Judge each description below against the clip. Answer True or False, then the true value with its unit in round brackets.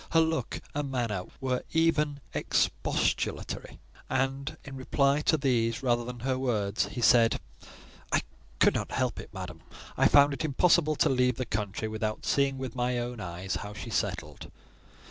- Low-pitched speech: True (125 Hz)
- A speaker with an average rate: True (160 wpm)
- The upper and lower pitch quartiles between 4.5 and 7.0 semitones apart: False (3.7 semitones)